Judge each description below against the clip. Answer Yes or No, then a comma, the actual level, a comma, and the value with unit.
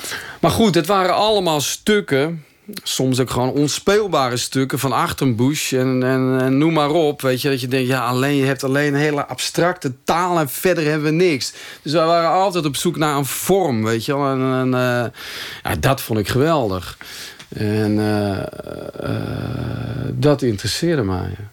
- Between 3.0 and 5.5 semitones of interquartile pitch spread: Yes, average, 4.2 semitones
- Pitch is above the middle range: No, low, 135 Hz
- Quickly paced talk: No, average, 165 wpm